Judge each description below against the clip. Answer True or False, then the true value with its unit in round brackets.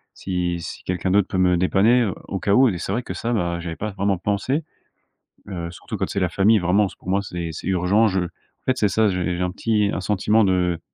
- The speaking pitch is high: False (95 Hz)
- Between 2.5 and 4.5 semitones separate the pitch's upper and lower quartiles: True (2.8 semitones)